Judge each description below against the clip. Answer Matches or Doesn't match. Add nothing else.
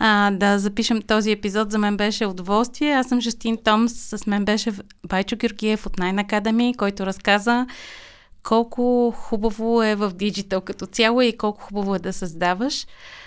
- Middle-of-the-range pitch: Doesn't match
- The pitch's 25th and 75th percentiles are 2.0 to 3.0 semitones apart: Matches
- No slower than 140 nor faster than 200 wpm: Matches